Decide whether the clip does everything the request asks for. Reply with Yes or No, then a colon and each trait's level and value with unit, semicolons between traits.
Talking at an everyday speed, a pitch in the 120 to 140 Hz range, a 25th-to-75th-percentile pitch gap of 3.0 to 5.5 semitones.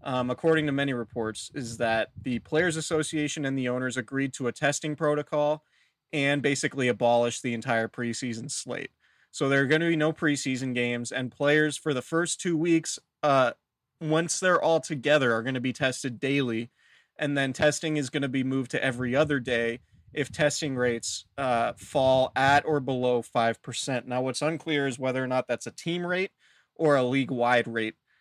Yes: average, 190 wpm; low, 135 Hz; average, 3.6 semitones